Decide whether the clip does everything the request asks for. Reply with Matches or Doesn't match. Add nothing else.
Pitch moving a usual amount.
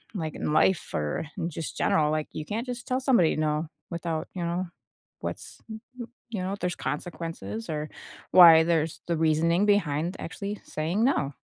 Matches